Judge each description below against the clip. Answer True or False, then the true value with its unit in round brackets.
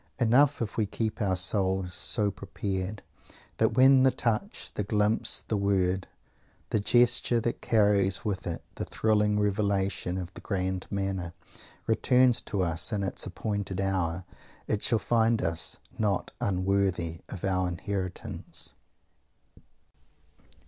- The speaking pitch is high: False (100 Hz)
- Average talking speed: False (130 wpm)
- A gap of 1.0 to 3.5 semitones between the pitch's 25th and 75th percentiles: True (2.8 semitones)